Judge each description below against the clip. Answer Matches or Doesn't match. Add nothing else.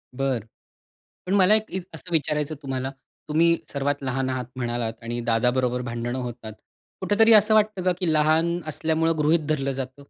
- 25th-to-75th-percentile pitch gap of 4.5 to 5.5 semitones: Matches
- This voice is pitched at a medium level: Matches